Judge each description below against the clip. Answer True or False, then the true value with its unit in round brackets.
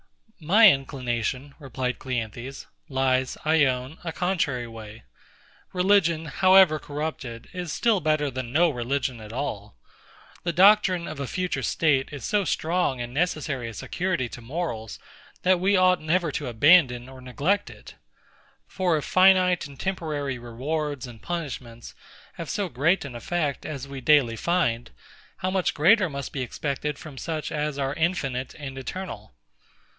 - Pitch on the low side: False (145 Hz)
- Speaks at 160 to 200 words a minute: False (150 wpm)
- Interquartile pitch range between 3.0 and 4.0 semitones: False (5.4 semitones)